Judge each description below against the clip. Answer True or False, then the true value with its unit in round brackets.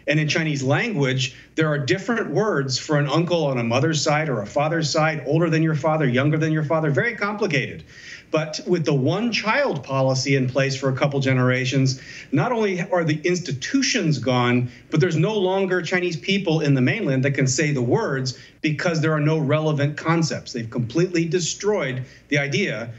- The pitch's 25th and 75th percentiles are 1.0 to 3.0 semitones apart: False (4.1 semitones)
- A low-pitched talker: False (155 Hz)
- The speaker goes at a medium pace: True (190 wpm)